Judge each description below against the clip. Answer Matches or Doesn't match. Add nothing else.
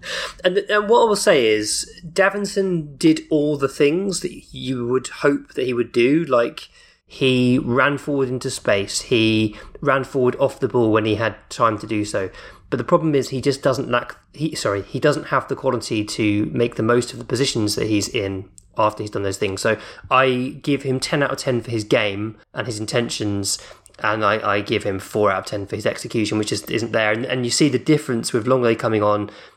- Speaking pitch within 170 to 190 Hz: Doesn't match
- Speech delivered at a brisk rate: Matches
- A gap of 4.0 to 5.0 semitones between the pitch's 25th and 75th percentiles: Matches